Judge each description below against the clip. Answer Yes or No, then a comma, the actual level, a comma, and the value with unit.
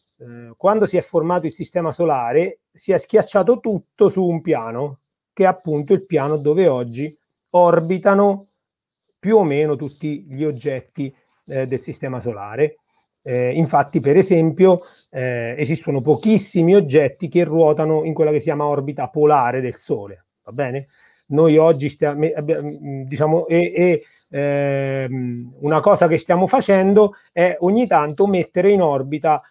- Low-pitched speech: No, medium, 155 Hz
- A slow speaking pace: No, average, 145 wpm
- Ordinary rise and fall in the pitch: Yes, average, 3.9 semitones